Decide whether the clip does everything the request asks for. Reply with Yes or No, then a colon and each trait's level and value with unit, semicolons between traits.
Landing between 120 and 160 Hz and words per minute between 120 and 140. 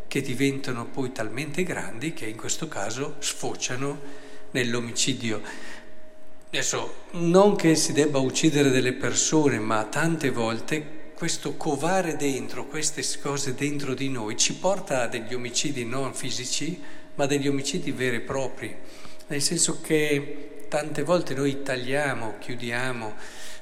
Yes: medium, 140 Hz; average, 130 wpm